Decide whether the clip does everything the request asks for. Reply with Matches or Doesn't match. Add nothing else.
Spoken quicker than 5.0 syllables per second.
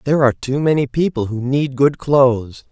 Matches